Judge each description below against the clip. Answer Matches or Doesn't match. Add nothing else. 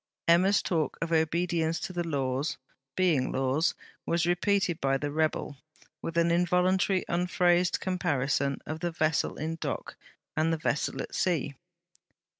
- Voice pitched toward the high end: Doesn't match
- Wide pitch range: Doesn't match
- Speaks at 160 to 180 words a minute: Doesn't match